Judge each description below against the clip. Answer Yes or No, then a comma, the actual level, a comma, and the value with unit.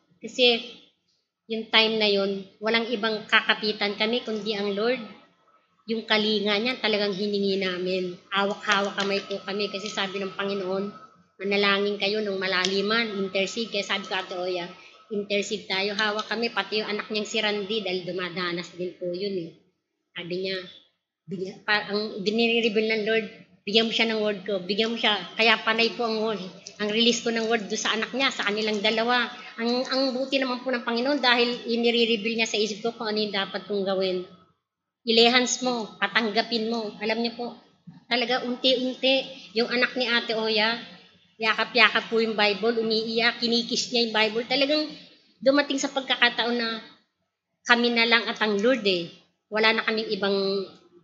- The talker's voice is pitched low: No, high, 215 Hz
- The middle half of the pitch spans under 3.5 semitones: Yes, average, 2.7 semitones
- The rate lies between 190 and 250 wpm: No, average, 165 wpm